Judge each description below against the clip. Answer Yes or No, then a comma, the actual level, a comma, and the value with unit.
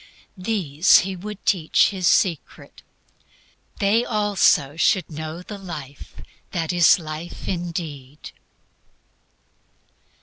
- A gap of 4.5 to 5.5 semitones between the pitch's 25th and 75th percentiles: No, average, 3.9 semitones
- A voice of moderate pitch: Yes, medium, 175 Hz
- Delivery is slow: Yes, slow, 95 wpm